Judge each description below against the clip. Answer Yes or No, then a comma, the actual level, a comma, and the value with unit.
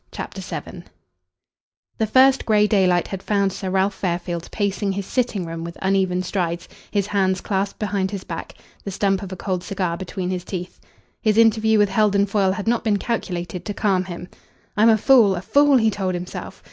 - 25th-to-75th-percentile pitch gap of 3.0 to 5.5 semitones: No, narrow, 2.4 semitones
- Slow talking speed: No, average, 190 wpm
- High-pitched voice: Yes, high, 195 Hz